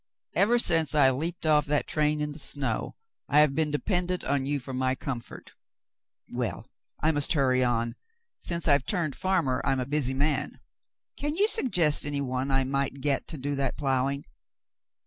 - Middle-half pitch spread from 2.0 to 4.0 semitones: Yes, average, 2.8 semitones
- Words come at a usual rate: Yes, average, 175 wpm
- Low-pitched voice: No, medium, 145 Hz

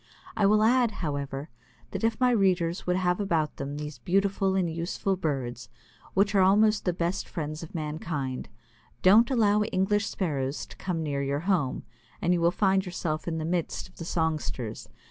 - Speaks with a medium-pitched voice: Yes, medium, 175 Hz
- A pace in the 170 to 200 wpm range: Yes, average, 185 wpm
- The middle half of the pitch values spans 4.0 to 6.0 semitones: Yes, average, 4.3 semitones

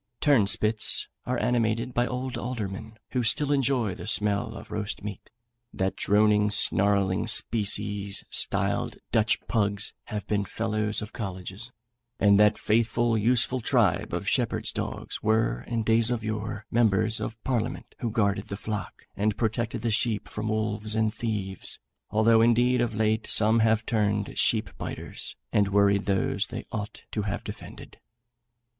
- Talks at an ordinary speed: Yes, average, 150 wpm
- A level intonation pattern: Yes, narrow, 2.0 semitones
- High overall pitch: No, low, 110 Hz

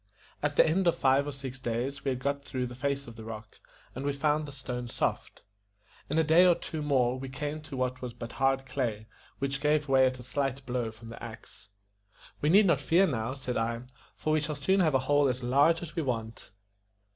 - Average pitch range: Yes, average, 3.2 semitones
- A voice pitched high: No, low, 135 Hz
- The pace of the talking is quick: Yes, fast, 230 wpm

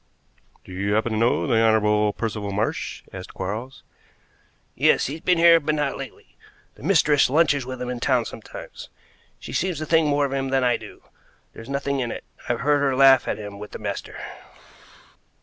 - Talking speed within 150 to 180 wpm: No, average, 190 wpm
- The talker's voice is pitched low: Yes, low, 130 Hz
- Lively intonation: No, average, 4.7 semitones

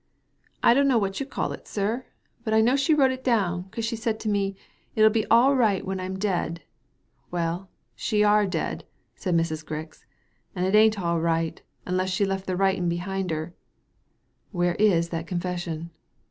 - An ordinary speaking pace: Yes, average, 190 wpm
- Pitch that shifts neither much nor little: Yes, average, 3.9 semitones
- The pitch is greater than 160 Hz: Yes, high, 190 Hz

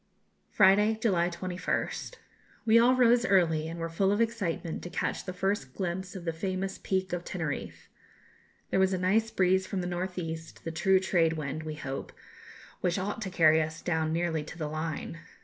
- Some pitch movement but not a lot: Yes, average, 3.0 semitones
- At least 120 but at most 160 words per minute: No, average, 185 wpm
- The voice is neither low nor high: Yes, medium, 180 Hz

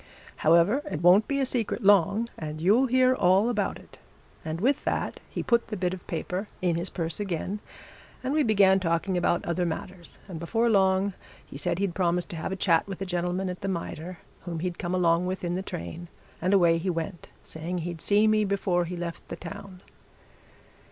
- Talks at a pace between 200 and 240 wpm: Yes, fast, 205 wpm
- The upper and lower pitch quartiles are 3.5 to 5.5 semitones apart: No, average, 2.8 semitones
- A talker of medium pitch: Yes, medium, 180 Hz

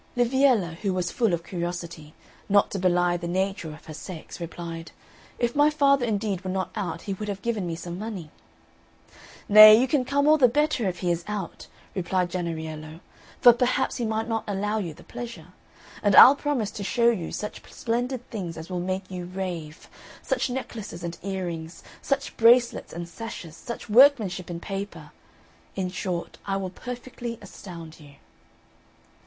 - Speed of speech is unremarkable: Yes, average, 170 wpm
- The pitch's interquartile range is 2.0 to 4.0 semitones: No, average, 5.2 semitones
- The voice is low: No, high, 195 Hz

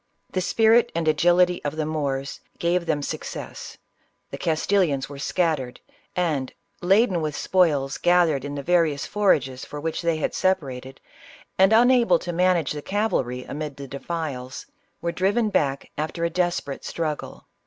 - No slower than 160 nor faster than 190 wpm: No, average, 150 wpm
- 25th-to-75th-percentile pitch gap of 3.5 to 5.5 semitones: Yes, average, 4.2 semitones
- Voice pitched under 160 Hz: No, medium, 165 Hz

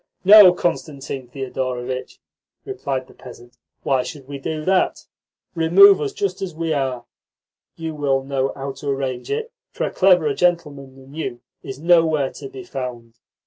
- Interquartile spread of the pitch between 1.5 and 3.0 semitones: No, average, 4.6 semitones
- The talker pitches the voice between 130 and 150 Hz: Yes, medium, 140 Hz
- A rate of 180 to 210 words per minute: No, average, 155 wpm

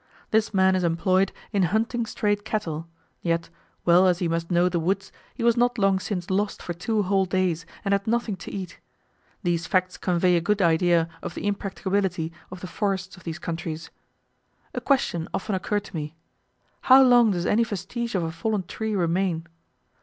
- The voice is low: No, medium, 185 Hz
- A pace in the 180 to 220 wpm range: Yes, average, 185 wpm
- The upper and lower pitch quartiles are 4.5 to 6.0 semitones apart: No, average, 3.2 semitones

